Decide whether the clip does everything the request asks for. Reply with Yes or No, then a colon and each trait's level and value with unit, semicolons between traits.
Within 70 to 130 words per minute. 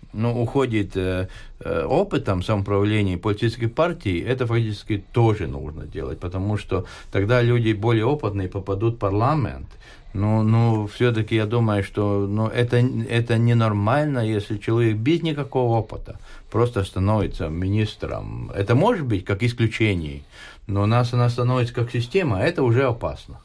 No: average, 145 wpm